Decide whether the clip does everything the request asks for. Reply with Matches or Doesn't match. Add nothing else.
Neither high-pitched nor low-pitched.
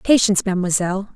Doesn't match